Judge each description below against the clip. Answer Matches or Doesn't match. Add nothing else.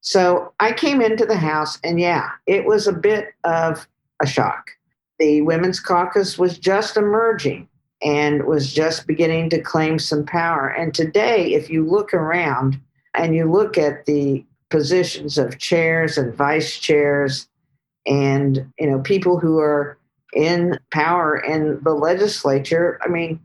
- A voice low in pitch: Doesn't match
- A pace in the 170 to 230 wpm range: Doesn't match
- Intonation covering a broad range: Doesn't match